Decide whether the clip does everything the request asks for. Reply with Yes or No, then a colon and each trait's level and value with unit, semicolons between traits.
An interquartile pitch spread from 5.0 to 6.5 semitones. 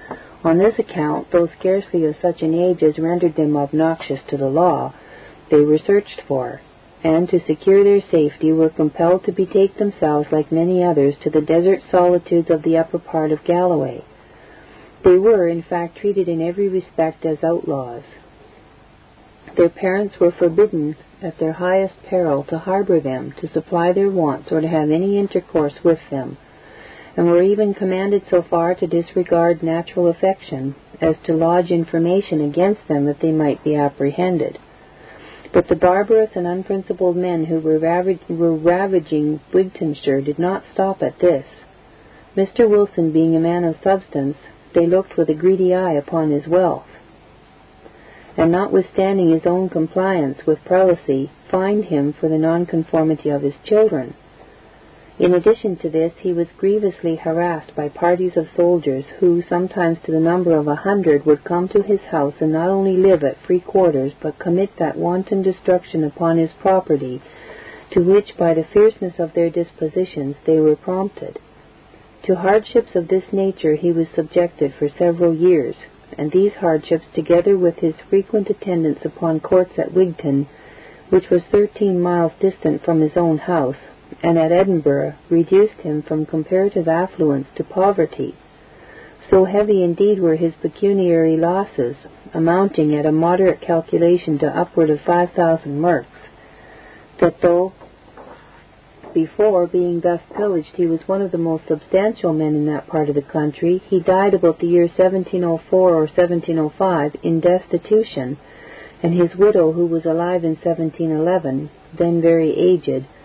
No: average, 3.0 semitones